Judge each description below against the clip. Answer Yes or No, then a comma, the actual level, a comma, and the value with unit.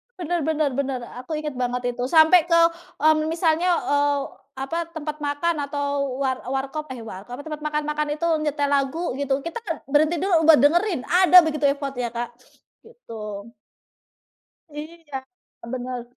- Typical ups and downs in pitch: Yes, average, 3.0 semitones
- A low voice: No, very high, 300 Hz